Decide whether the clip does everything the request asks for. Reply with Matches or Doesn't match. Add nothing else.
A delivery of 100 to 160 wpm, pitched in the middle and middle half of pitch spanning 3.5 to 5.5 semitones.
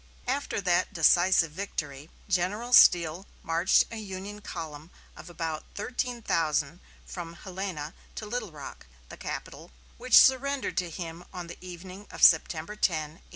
Matches